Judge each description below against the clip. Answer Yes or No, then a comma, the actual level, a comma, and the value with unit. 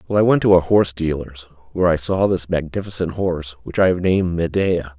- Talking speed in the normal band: No, fast, 215 wpm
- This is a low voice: Yes, very low, 85 Hz